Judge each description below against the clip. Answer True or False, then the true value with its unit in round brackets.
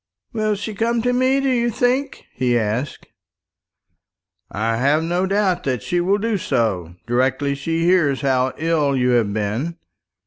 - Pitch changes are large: True (8.7 semitones)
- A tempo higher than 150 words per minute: True (160 wpm)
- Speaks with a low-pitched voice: False (155 Hz)